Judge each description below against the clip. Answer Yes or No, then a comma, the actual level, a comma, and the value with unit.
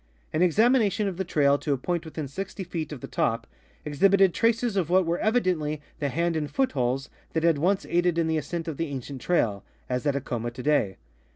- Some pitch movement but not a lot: Yes, average, 4.7 semitones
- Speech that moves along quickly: Yes, fast, 215 wpm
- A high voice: No, medium, 160 Hz